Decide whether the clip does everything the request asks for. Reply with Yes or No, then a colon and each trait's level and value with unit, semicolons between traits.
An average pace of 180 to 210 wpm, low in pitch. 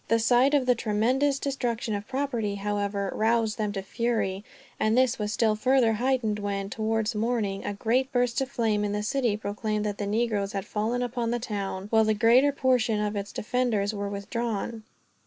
No: average, 190 wpm; high, 220 Hz